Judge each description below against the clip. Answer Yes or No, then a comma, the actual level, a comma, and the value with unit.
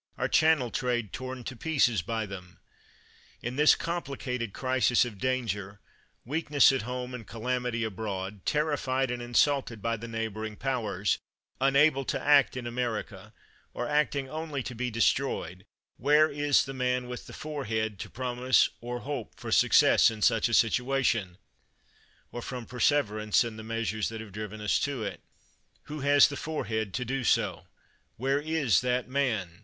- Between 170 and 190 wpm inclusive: No, average, 160 wpm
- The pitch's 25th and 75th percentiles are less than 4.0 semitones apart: Yes, average, 3.6 semitones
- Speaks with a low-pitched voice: Yes, low, 125 Hz